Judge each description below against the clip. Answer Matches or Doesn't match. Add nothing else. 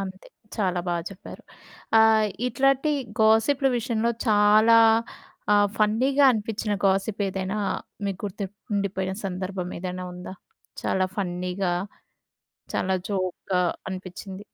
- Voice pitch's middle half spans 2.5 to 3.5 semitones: Matches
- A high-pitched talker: Matches